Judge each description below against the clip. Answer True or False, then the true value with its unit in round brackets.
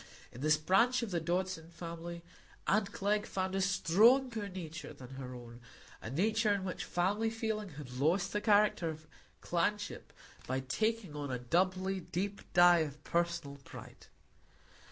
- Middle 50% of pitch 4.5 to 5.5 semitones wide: True (4.8 semitones)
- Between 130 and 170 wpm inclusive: True (155 wpm)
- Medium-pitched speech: True (180 Hz)